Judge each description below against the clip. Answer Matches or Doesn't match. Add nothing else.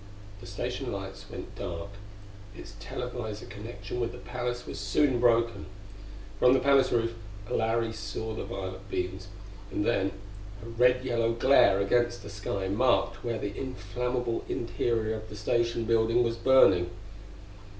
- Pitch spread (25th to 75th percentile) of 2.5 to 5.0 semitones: Matches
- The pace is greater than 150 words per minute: Doesn't match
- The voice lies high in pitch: Doesn't match